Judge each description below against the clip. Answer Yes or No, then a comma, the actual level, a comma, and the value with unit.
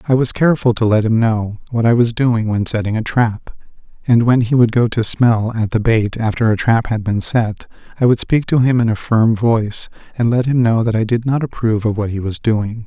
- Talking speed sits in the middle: No, fast, 250 wpm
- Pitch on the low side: Yes, low, 115 Hz